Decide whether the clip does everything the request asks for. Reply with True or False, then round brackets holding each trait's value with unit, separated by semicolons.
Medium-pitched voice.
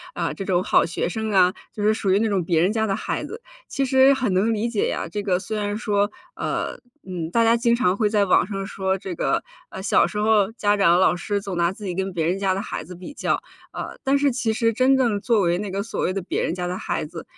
False (200 Hz)